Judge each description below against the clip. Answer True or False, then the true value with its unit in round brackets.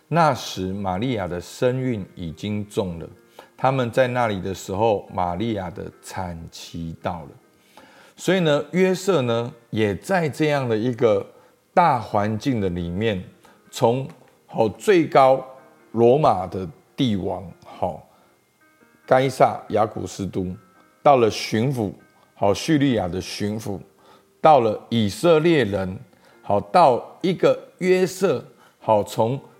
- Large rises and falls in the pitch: True (5.9 semitones)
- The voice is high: False (115 Hz)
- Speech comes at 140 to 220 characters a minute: True (180 characters per minute)